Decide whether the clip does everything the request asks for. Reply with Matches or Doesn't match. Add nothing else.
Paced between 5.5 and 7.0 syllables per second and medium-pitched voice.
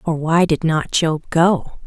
Doesn't match